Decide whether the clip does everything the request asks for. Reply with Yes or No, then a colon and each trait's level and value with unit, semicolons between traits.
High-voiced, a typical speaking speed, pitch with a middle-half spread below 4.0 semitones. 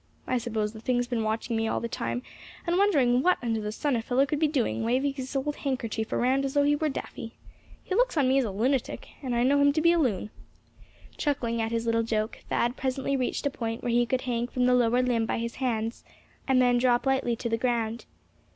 No: high, 245 Hz; fast, 240 wpm; average, 2.9 semitones